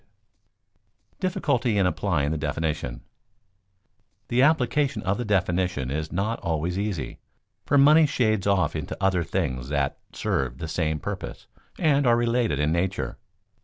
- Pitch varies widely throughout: Yes, wide, 7.4 semitones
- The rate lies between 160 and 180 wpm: No, average, 140 wpm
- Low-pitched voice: Yes, very low, 95 Hz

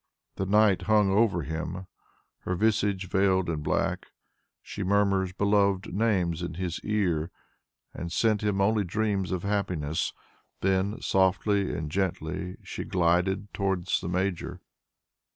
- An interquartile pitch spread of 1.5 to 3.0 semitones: Yes, narrow, 2.4 semitones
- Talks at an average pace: No, slow, 130 wpm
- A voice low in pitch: Yes, very low, 95 Hz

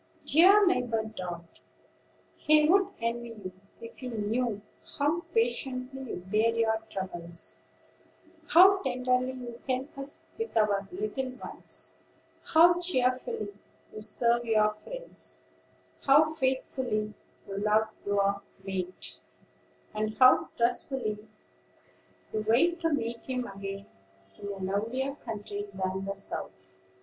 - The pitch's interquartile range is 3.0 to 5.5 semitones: Yes, average, 4.5 semitones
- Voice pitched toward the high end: Yes, high, 235 Hz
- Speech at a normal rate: No, slow, 120 wpm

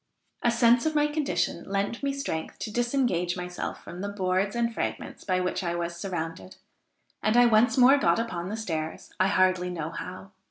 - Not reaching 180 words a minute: No, average, 190 wpm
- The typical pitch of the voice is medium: No, high, 195 Hz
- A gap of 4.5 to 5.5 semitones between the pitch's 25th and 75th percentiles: Yes, average, 5.1 semitones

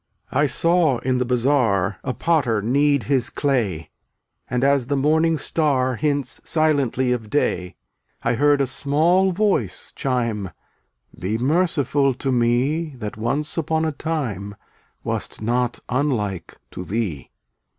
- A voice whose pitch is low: Yes, low, 130 Hz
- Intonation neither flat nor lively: Yes, average, 4.1 semitones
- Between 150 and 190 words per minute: No, average, 140 wpm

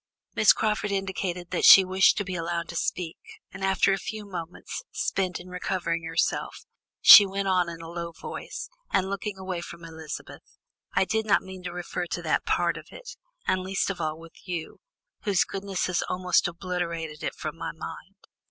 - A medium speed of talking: Yes, average, 190 wpm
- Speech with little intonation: Yes, narrow, 2.3 semitones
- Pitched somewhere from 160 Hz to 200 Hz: Yes, medium, 185 Hz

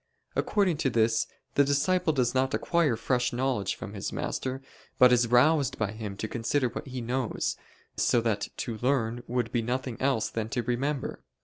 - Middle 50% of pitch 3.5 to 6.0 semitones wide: No, average, 2.8 semitones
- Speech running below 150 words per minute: No, average, 180 wpm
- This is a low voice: Yes, low, 125 Hz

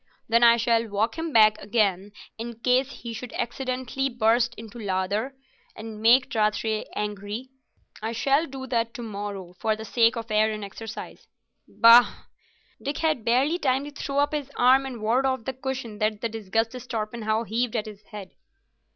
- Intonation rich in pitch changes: No, average, 3.0 semitones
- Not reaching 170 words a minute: No, average, 175 wpm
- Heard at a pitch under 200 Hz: No, high, 230 Hz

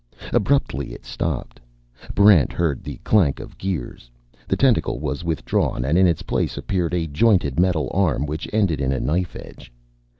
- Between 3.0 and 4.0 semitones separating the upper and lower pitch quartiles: No, average, 4.7 semitones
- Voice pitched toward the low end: Yes, very low, 80 Hz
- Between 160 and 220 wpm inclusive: Yes, average, 165 wpm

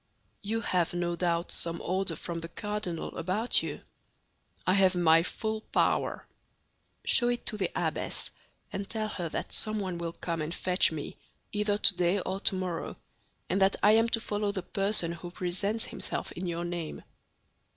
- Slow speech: No, average, 165 wpm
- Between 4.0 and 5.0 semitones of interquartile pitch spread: No, average, 3.3 semitones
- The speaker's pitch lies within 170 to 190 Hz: Yes, medium, 185 Hz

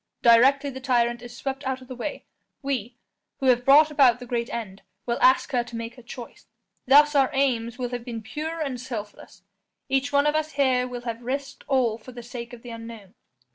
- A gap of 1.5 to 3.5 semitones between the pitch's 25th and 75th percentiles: Yes, narrow, 2.4 semitones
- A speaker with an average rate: No, fast, 215 wpm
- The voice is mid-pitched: No, very high, 250 Hz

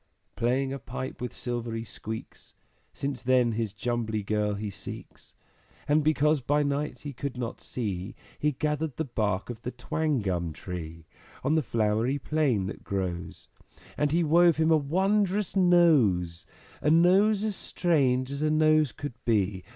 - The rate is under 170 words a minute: Yes, average, 155 wpm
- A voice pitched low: Yes, low, 130 Hz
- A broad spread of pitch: Yes, wide, 6.2 semitones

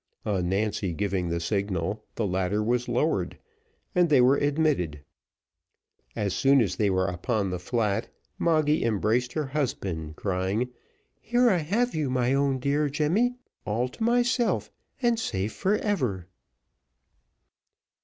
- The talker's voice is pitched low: Yes, low, 120 Hz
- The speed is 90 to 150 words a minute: Yes, slow, 135 wpm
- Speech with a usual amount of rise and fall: No, wide, 7.7 semitones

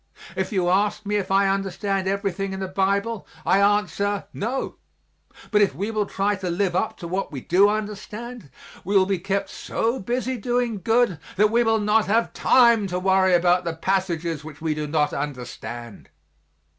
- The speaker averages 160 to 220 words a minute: Yes, average, 180 wpm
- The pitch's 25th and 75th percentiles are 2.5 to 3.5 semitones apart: Yes, average, 2.8 semitones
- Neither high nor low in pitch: No, high, 195 Hz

